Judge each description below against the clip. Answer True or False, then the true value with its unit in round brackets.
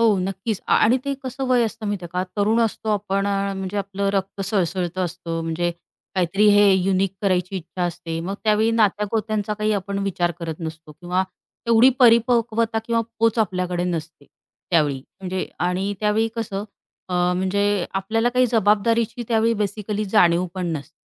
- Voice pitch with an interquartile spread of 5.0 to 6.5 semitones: False (3.3 semitones)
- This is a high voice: True (200 Hz)